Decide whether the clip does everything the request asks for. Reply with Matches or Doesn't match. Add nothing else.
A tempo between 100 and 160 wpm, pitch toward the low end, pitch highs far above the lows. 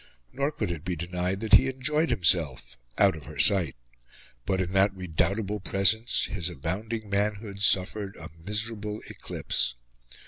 Doesn't match